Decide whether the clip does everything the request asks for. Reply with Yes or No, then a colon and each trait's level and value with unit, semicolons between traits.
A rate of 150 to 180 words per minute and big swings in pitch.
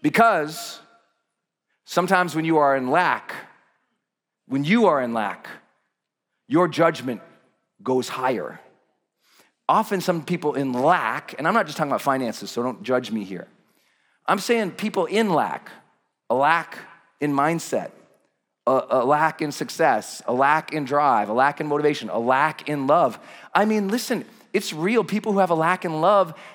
Yes: average, 160 wpm; wide, 5.9 semitones